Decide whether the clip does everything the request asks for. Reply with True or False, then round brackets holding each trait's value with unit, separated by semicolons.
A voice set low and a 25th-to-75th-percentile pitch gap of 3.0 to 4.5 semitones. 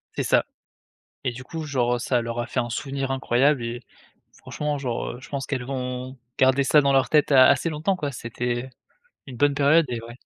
False (130 Hz; 2.6 semitones)